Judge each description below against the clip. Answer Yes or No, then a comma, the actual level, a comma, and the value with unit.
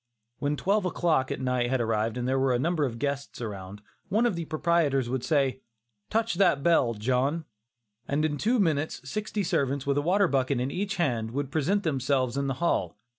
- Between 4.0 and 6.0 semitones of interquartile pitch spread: Yes, average, 5.0 semitones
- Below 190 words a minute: No, average, 200 wpm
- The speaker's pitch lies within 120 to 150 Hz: Yes, medium, 140 Hz